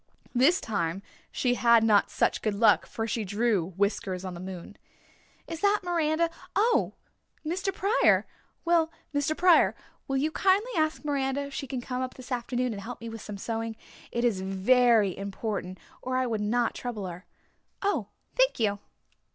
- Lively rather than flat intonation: Yes, wide, 6.8 semitones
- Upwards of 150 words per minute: Yes, average, 170 wpm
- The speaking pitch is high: Yes, high, 240 Hz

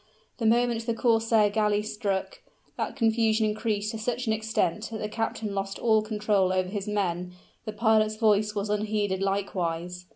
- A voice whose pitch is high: Yes, high, 215 Hz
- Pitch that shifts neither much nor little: No, narrow, 1.9 semitones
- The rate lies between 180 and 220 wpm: No, average, 165 wpm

